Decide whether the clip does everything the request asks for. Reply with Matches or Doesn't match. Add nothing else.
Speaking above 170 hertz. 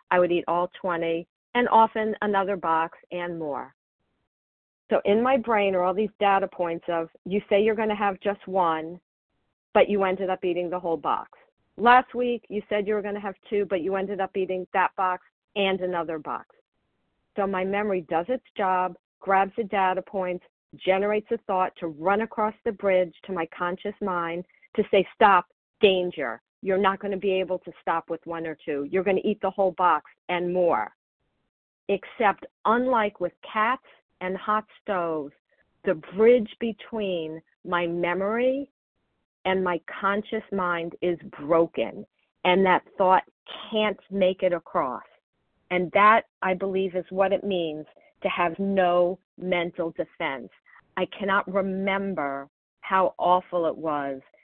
Matches